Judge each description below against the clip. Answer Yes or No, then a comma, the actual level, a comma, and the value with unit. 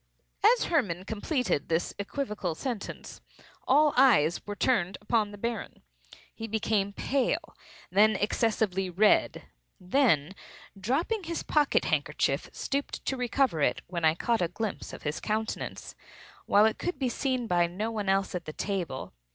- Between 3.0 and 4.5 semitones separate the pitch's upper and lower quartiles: No, wide, 5.6 semitones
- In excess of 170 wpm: No, average, 150 wpm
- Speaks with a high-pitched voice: Yes, high, 215 Hz